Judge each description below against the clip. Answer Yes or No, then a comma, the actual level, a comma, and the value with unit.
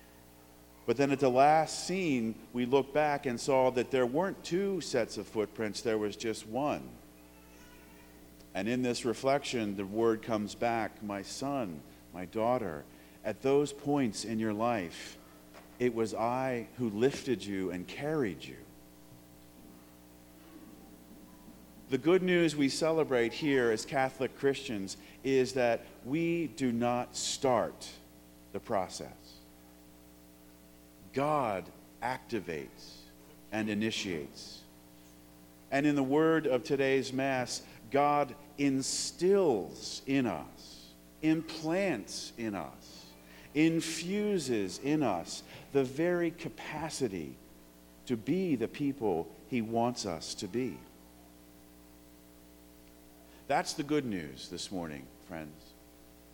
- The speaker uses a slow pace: Yes, slow, 115 wpm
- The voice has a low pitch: Yes, low, 105 Hz